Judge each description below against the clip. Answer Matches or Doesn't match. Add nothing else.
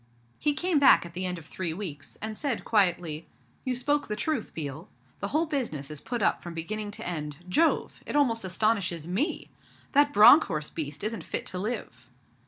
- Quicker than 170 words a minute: Matches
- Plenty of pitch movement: Matches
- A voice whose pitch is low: Doesn't match